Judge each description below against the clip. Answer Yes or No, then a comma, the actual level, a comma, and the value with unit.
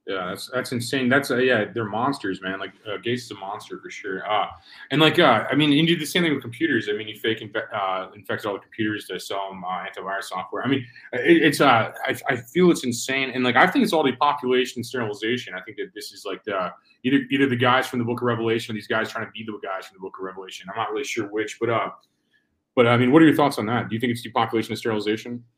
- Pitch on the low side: Yes, low, 120 Hz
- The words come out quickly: Yes, fast, 275 wpm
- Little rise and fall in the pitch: No, average, 3.8 semitones